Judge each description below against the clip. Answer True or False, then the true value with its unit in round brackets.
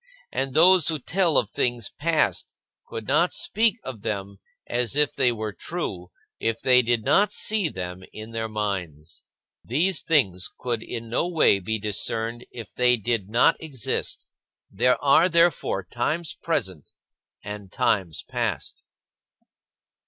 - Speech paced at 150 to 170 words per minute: False (140 wpm)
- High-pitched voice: False (120 Hz)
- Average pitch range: False (6.8 semitones)